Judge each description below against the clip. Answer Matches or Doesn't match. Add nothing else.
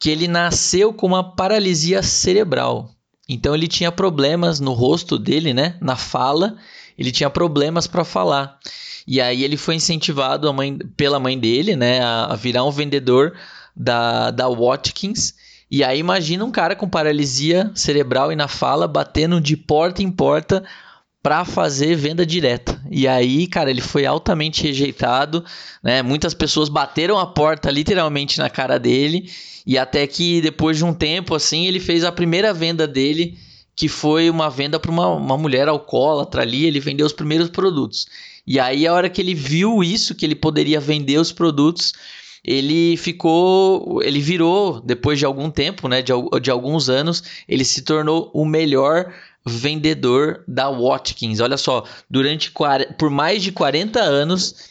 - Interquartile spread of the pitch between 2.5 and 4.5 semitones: Matches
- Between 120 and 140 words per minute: Doesn't match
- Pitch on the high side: Doesn't match